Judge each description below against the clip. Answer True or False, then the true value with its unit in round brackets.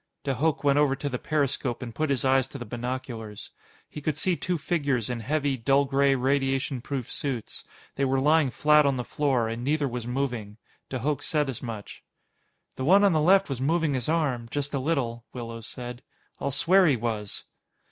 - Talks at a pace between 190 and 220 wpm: True (200 wpm)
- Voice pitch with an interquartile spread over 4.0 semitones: False (3.3 semitones)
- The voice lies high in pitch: False (135 Hz)